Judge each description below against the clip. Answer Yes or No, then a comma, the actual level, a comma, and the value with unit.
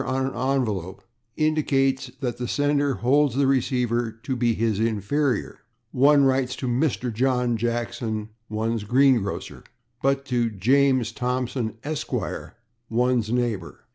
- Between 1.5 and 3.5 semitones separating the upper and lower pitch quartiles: Yes, average, 2.9 semitones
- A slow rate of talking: Yes, slow, 130 wpm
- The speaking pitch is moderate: No, low, 125 Hz